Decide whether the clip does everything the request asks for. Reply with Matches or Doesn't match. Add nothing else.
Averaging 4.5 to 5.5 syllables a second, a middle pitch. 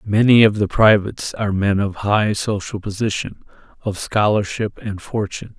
Doesn't match